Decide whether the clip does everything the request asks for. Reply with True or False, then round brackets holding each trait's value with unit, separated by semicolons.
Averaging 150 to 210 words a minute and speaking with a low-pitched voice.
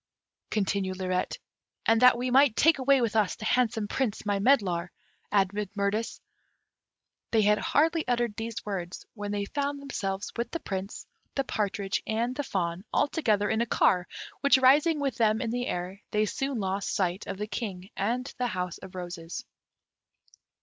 False (170 wpm; 215 Hz)